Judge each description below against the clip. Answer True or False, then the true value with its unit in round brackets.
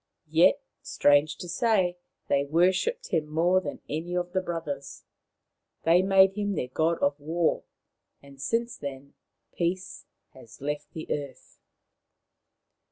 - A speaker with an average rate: False (130 wpm)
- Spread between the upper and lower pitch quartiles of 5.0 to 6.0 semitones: False (4.3 semitones)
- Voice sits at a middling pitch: True (165 Hz)